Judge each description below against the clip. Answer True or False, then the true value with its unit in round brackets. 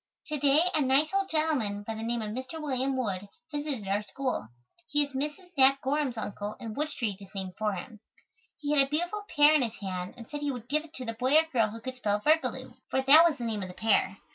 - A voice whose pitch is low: False (260 Hz)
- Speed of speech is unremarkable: False (250 wpm)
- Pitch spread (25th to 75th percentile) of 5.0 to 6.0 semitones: True (5.5 semitones)